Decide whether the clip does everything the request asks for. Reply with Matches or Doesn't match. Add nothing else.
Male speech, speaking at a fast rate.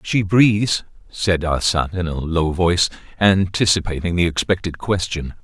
Doesn't match